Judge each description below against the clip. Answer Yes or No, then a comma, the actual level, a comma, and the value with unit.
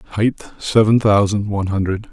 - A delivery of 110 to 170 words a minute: Yes, average, 140 wpm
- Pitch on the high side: No, low, 105 Hz